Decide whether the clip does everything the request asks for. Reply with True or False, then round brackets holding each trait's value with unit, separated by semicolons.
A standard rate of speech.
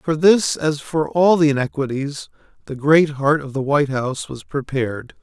True (185 wpm)